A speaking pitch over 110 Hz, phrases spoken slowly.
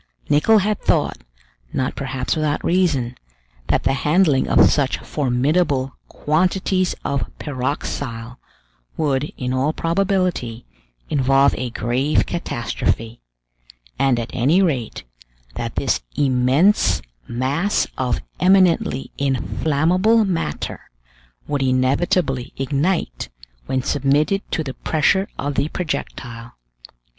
Yes: medium, 140 Hz; slow, 105 wpm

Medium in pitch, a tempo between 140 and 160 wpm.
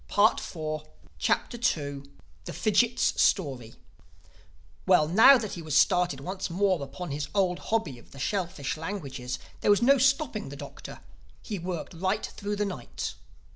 Yes: medium, 180 Hz; average, 150 wpm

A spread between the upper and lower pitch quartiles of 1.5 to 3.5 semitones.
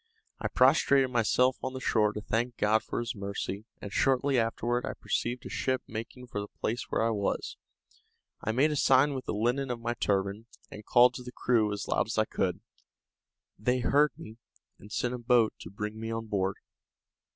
Yes: average, 2.9 semitones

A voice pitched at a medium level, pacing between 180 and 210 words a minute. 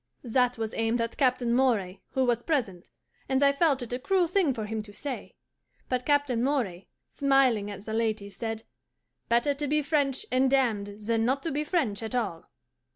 No: very high, 250 Hz; average, 190 wpm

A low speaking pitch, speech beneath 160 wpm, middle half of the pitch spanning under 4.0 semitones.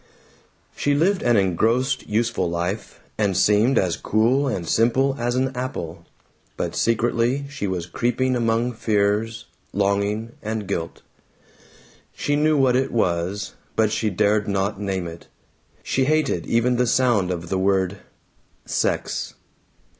No: low, 110 Hz; slow, 135 wpm; average, 4.3 semitones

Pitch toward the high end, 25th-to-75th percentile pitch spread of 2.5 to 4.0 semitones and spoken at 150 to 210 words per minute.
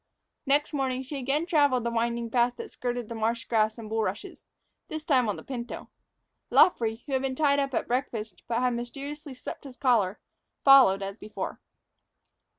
Yes: high, 245 Hz; average, 3.2 semitones; average, 175 wpm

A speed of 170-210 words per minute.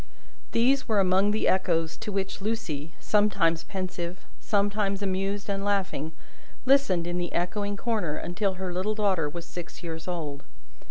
No: average, 150 wpm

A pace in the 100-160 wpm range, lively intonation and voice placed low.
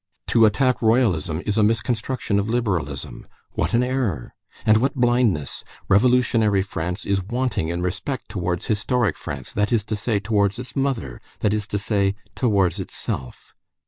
No: average, 155 wpm; average, 4.3 semitones; low, 105 Hz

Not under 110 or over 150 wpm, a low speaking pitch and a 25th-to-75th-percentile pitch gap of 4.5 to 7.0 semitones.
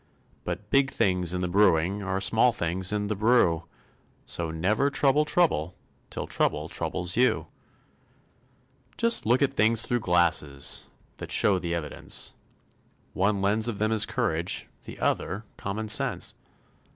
Yes: average, 140 wpm; low, 100 Hz; average, 4.8 semitones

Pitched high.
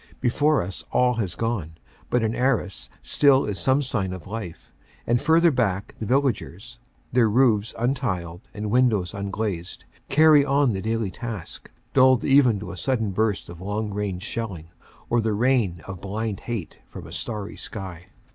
No: low, 110 Hz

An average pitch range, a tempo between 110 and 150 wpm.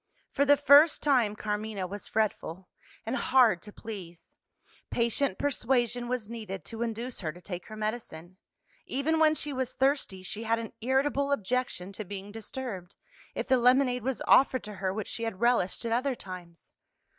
No: average, 4.8 semitones; average, 170 wpm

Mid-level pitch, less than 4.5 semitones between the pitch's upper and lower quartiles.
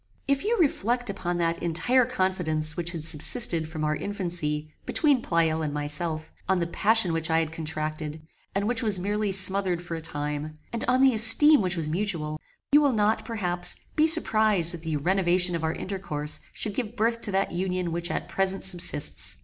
No: medium, 180 Hz; average, 5.0 semitones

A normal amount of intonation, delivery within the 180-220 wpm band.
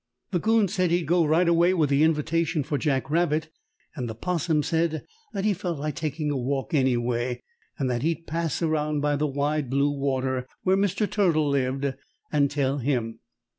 Yes: average, 3.5 semitones; average, 185 wpm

